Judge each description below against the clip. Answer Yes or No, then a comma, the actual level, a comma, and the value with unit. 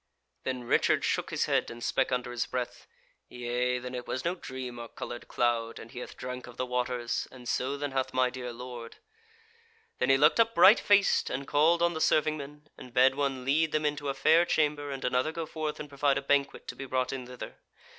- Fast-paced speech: Yes, fast, 225 wpm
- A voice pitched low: Yes, low, 130 Hz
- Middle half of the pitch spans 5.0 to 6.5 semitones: No, average, 2.9 semitones